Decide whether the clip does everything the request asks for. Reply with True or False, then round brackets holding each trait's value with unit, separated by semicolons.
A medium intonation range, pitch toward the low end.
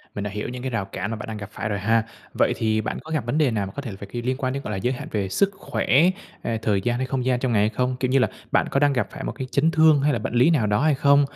True (4.4 semitones; 120 Hz)